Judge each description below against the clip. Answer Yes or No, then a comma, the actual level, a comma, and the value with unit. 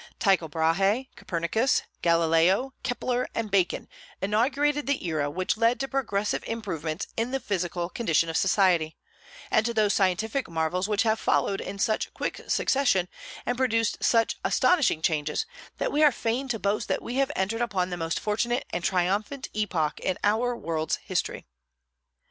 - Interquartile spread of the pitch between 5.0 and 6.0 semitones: Yes, wide, 5.5 semitones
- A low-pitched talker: No, high, 205 Hz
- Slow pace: No, average, 160 wpm